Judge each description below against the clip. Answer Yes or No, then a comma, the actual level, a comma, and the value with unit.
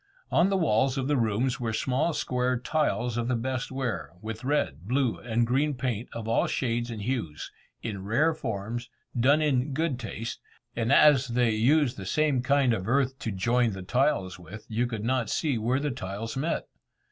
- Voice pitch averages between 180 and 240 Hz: No, low, 120 Hz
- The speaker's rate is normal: Yes, average, 190 wpm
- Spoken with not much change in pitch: No, average, 3.3 semitones